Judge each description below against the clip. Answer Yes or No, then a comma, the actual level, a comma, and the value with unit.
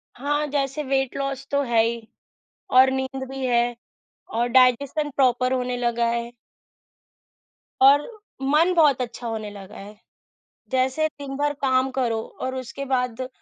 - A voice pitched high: Yes, very high, 260 Hz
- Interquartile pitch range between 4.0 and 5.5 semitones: No, narrow, 2.4 semitones